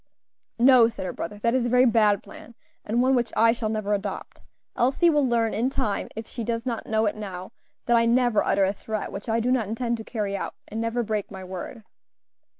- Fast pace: Yes, fast, 230 wpm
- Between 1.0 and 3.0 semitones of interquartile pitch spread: Yes, narrow, 2.5 semitones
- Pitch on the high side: Yes, high, 225 Hz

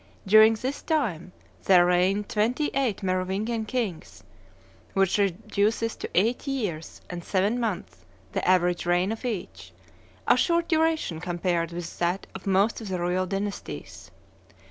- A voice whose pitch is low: No, high, 195 Hz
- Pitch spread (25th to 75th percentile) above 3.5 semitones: Yes, average, 4.2 semitones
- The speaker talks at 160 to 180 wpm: No, average, 140 wpm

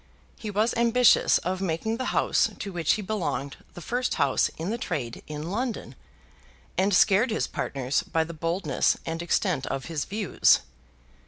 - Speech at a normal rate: Yes, average, 165 wpm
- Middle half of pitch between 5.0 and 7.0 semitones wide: Yes, average, 5.3 semitones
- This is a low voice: No, medium, 185 Hz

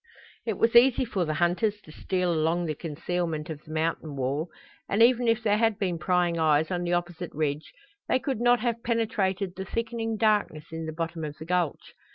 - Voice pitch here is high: No, medium, 175 Hz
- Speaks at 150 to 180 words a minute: No, fast, 205 wpm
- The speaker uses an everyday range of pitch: No, wide, 5.7 semitones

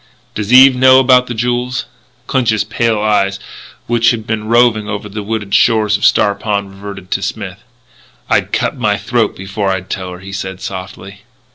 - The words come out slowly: No, average, 175 wpm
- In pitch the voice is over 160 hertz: No, low, 105 Hz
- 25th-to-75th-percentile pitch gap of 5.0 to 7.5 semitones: No, average, 3.2 semitones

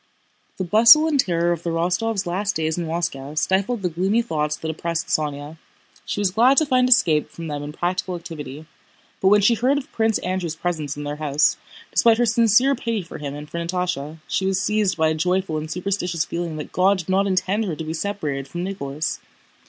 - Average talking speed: No, fast, 210 wpm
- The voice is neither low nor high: Yes, medium, 175 Hz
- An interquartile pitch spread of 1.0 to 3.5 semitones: No, average, 4.5 semitones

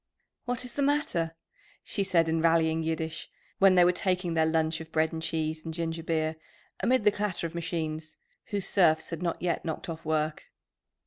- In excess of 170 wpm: Yes, average, 190 wpm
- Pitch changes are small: Yes, narrow, 2.1 semitones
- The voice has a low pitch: No, medium, 165 Hz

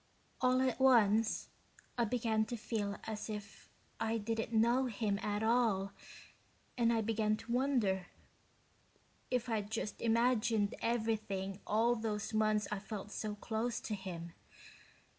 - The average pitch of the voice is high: Yes, high, 220 Hz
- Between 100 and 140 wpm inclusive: Yes, slow, 135 wpm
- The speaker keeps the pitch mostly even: Yes, narrow, 2.1 semitones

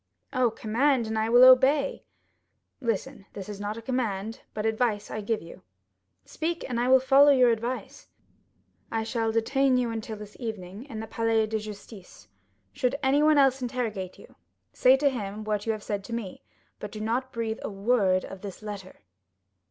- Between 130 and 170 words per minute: No, average, 180 wpm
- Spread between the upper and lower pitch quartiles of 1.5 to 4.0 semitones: Yes, average, 3.3 semitones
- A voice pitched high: Yes, high, 225 Hz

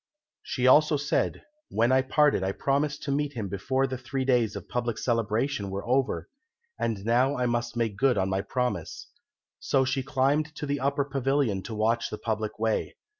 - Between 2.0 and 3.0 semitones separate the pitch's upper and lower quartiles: No, average, 3.7 semitones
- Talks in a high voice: No, low, 125 Hz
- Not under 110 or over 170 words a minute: No, average, 180 wpm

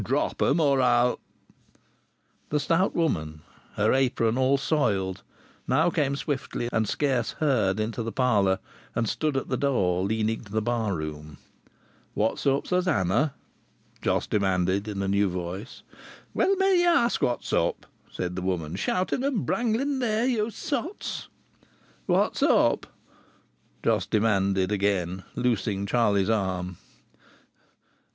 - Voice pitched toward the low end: Yes, low, 110 Hz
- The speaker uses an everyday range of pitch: No, wide, 7.0 semitones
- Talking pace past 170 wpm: No, slow, 135 wpm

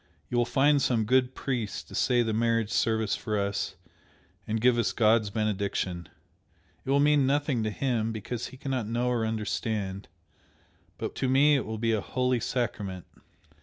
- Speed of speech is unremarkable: Yes, average, 170 wpm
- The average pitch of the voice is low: Yes, low, 115 Hz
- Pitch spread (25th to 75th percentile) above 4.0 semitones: No, average, 3.0 semitones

